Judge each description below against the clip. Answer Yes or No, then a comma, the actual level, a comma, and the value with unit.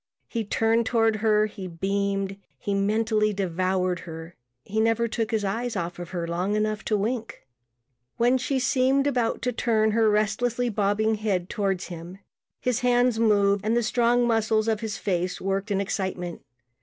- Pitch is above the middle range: Yes, high, 215 Hz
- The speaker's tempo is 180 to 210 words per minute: No, average, 165 wpm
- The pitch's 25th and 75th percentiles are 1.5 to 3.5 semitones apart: Yes, average, 2.9 semitones